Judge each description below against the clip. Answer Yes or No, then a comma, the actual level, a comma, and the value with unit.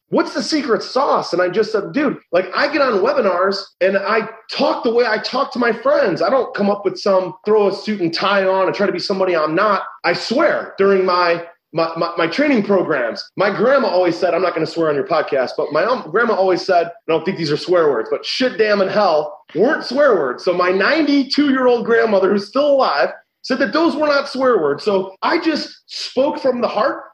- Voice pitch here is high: Yes, high, 205 Hz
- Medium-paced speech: No, fast, 235 wpm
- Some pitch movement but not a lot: No, wide, 7.0 semitones